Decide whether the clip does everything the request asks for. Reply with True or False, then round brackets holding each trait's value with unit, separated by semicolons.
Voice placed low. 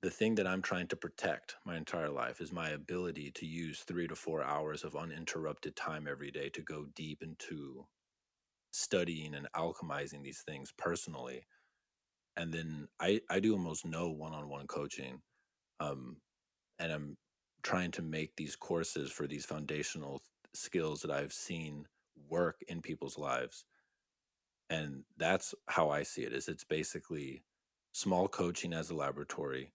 True (75 Hz)